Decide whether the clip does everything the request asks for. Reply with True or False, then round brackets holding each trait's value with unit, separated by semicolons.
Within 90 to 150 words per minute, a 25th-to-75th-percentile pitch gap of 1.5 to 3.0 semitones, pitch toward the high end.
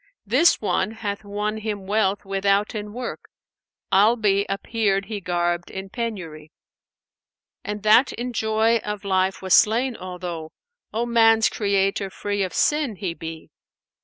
True (140 wpm; 2.6 semitones; 205 Hz)